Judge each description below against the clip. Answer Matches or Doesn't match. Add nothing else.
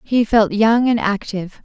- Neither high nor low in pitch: Doesn't match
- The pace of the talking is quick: Doesn't match